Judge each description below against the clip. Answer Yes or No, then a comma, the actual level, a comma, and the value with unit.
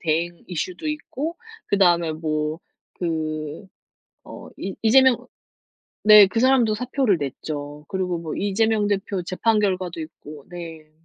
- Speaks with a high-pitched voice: No, medium, 180 Hz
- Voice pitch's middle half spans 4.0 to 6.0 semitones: Yes, average, 5.2 semitones